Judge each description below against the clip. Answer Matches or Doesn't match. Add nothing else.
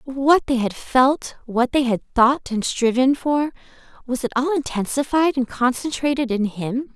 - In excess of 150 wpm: Doesn't match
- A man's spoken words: Doesn't match